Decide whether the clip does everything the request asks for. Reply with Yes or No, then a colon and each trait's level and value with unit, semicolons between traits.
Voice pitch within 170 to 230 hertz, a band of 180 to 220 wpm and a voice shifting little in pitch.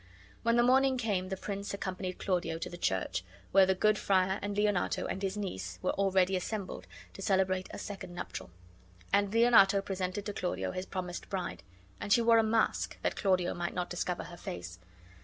Yes: high, 190 Hz; average, 190 wpm; narrow, 2.1 semitones